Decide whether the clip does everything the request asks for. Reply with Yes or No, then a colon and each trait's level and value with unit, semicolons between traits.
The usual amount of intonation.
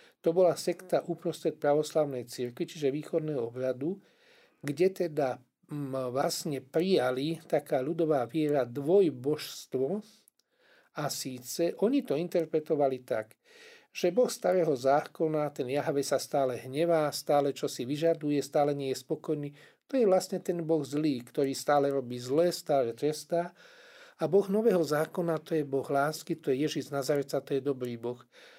Yes: average, 4.0 semitones